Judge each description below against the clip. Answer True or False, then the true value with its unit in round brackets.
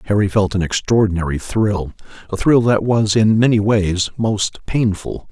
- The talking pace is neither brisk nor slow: True (160 wpm)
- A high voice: False (105 Hz)